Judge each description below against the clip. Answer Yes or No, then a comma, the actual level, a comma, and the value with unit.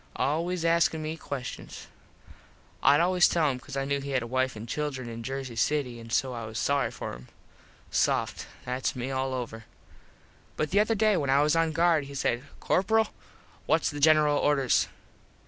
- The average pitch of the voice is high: No, medium, 140 Hz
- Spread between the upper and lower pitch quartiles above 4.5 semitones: No, average, 3.9 semitones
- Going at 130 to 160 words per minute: No, average, 185 wpm